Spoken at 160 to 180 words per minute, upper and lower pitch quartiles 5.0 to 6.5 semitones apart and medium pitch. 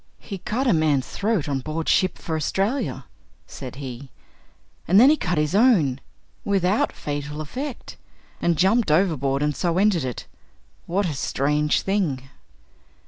No: average, 145 wpm; wide, 5.5 semitones; medium, 165 Hz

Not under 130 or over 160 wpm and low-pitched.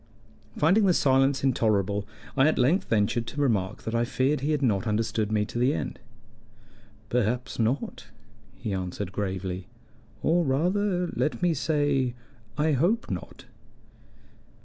Yes: average, 140 wpm; low, 130 Hz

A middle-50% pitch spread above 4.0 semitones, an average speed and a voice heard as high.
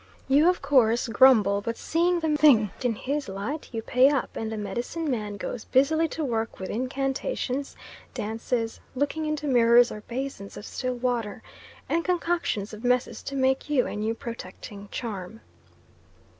Yes: average, 4.4 semitones; average, 160 wpm; very high, 250 Hz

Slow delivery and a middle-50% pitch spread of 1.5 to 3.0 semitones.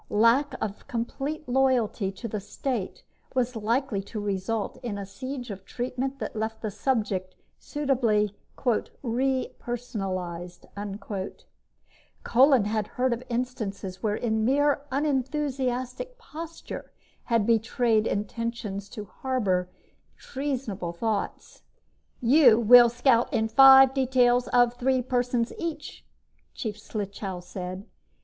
No: slow, 110 wpm; average, 3.9 semitones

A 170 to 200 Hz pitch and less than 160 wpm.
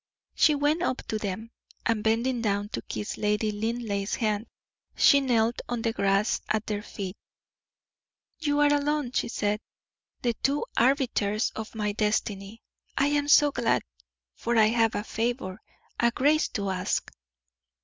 No: high, 225 Hz; average, 150 wpm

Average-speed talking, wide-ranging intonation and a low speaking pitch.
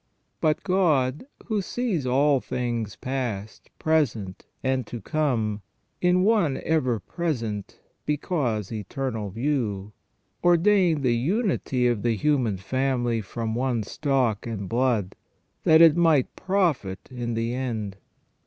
No: slow, 120 wpm; wide, 5.7 semitones; low, 130 Hz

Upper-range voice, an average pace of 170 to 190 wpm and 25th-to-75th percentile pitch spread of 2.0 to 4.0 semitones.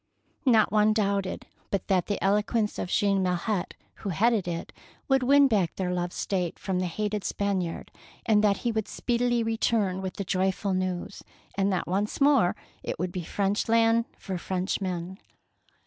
Yes: high, 200 Hz; average, 175 wpm; average, 3.0 semitones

